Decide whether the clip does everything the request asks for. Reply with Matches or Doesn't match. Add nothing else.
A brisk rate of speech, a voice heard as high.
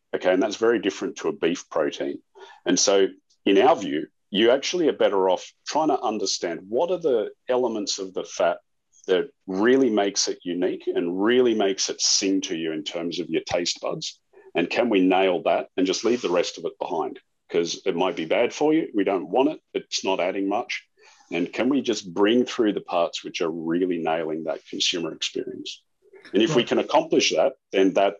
Matches